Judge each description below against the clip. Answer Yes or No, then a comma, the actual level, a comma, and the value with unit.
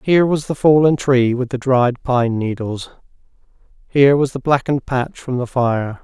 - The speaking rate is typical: Yes, average, 180 wpm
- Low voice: Yes, low, 130 Hz